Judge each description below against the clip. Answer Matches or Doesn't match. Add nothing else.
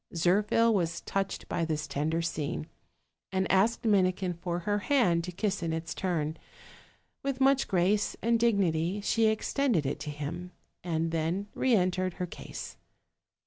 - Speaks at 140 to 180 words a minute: Matches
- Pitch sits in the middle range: Matches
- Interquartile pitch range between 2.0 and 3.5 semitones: Doesn't match